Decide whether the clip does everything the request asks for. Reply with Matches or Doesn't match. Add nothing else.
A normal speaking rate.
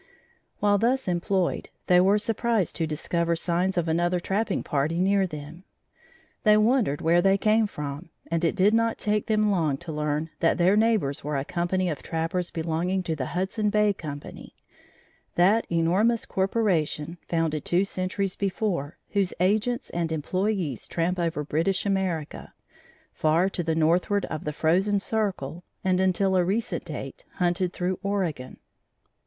Matches